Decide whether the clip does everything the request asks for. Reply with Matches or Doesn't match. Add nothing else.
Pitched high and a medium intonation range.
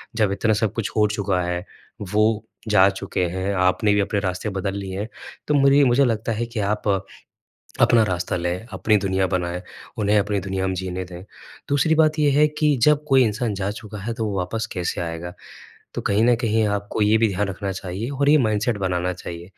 Doesn't match